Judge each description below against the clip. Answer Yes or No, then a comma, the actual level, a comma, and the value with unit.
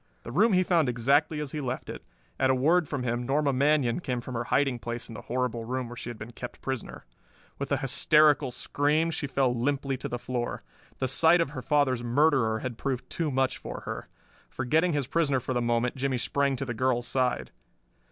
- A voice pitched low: Yes, low, 130 Hz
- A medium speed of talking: No, fast, 215 wpm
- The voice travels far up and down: No, average, 3.1 semitones